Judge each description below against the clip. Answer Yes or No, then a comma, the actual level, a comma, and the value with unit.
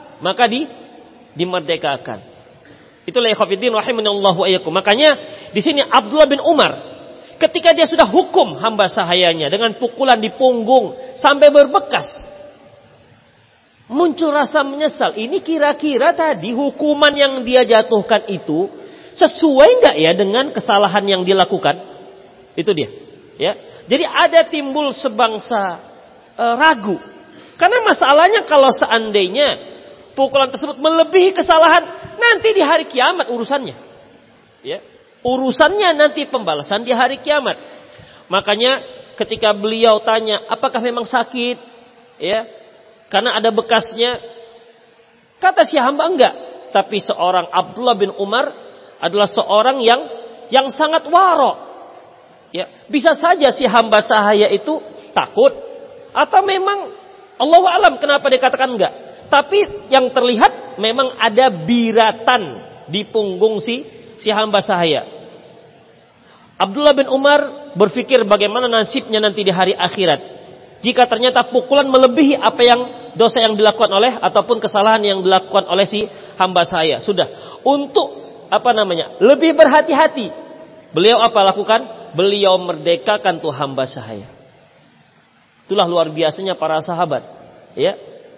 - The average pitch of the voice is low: No, high, 245 Hz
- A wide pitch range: Yes, wide, 6.2 semitones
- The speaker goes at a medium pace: Yes, average, 120 wpm